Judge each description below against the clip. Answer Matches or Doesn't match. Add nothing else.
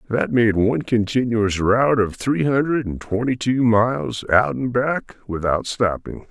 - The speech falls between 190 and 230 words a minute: Doesn't match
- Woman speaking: Doesn't match